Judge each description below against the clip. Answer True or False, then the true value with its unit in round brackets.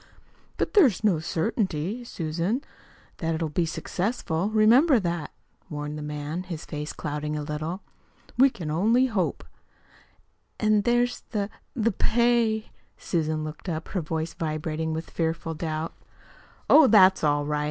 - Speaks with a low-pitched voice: False (170 Hz)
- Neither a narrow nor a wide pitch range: False (5.8 semitones)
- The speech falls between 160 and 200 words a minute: False (140 wpm)